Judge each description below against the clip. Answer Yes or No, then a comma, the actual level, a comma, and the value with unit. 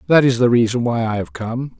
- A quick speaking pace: Yes, fast, 265 wpm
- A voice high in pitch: No, low, 120 Hz